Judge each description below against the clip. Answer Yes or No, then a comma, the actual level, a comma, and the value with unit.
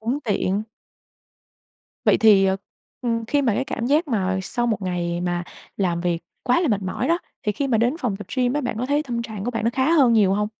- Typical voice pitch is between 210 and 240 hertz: Yes, high, 225 Hz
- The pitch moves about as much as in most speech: Yes, average, 4.7 semitones